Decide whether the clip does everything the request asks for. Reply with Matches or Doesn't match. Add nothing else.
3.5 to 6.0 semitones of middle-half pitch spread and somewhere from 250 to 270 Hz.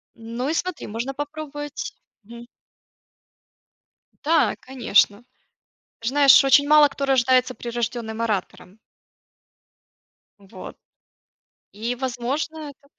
Matches